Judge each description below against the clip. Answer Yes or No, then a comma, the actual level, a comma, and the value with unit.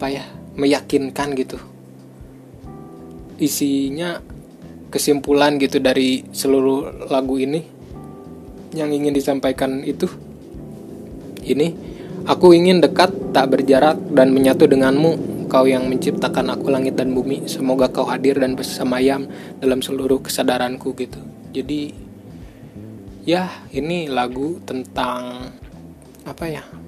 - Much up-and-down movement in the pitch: No, narrow, 2.4 semitones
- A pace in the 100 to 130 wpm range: Yes, average, 105 wpm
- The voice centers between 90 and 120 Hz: No, low, 135 Hz